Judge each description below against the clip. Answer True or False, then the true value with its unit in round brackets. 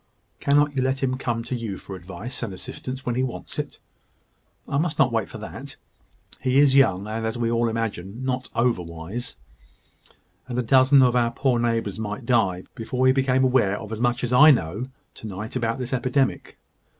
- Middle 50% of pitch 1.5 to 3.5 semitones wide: True (2.8 semitones)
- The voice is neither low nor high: False (120 Hz)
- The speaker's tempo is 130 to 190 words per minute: False (200 wpm)